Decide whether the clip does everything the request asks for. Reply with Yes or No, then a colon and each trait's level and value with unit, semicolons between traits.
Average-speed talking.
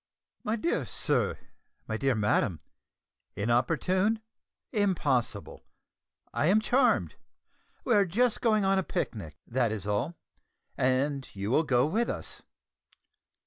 No: slow, 120 wpm